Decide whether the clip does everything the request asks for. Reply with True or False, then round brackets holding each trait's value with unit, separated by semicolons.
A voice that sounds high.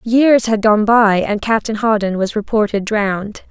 True (215 Hz)